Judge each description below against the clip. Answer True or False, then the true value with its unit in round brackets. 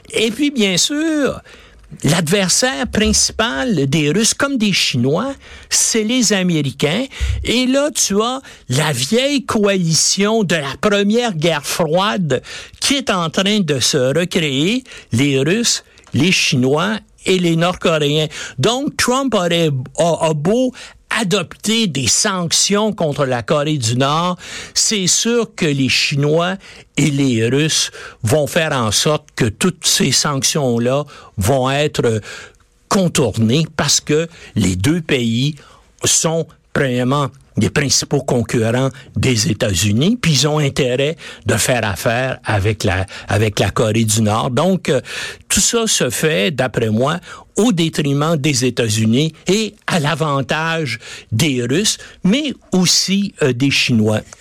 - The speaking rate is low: True (135 wpm)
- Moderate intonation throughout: False (7.1 semitones)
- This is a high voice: False (155 Hz)